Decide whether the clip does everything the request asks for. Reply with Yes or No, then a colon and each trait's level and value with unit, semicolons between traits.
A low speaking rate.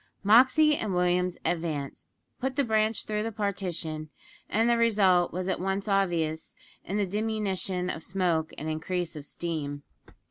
No: average, 150 wpm